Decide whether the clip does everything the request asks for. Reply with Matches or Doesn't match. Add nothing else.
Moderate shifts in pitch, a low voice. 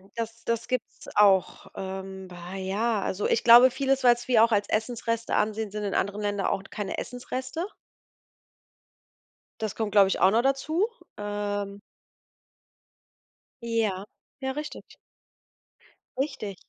Doesn't match